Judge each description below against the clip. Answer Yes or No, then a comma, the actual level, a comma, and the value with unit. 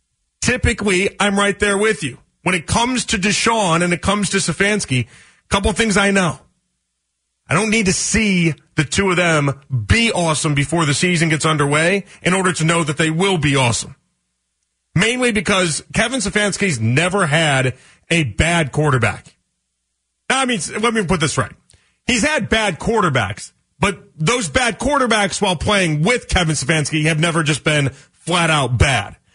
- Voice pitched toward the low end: No, medium, 170 Hz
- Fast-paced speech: No, average, 170 wpm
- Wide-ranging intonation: Yes, wide, 6.0 semitones